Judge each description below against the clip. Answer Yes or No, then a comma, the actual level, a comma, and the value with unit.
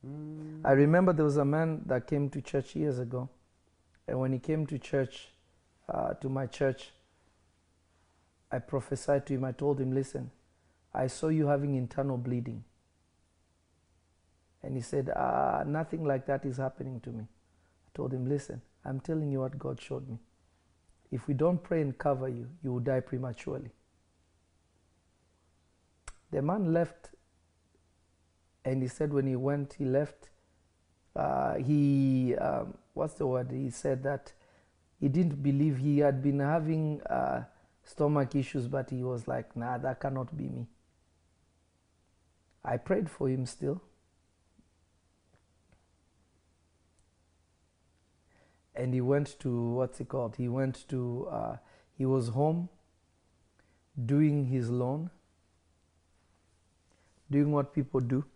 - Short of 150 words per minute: Yes, average, 140 wpm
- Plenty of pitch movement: Yes, wide, 8.8 semitones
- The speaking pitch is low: Yes, low, 125 Hz